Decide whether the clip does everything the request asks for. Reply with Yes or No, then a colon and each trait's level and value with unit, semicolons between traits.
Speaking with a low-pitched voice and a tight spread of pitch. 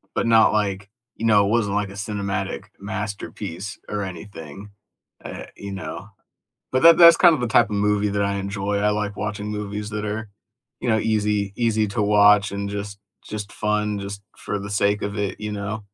Yes: low, 105 Hz; narrow, 1.0 semitones